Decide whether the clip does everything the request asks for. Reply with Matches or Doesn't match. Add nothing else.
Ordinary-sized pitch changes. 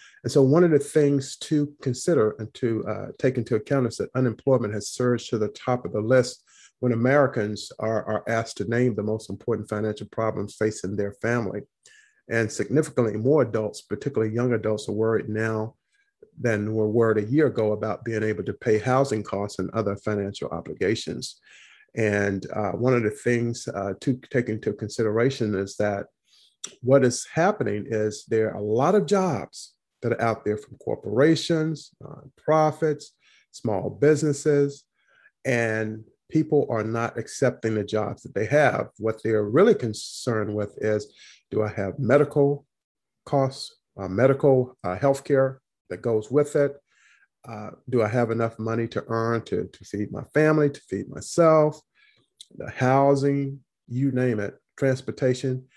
Matches